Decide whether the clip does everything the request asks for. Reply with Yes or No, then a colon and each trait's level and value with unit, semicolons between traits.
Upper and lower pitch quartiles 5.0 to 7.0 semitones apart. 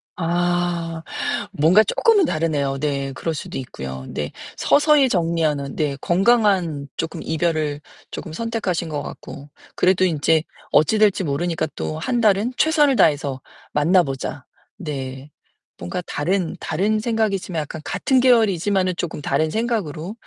Yes: wide, 5.6 semitones